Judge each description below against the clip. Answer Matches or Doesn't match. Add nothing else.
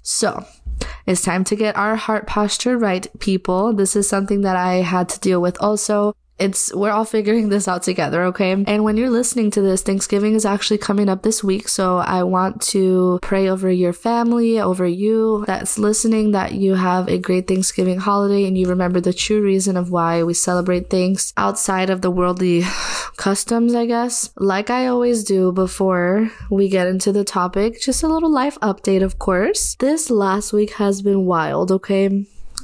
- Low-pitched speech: Doesn't match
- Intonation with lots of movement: Doesn't match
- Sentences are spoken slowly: Doesn't match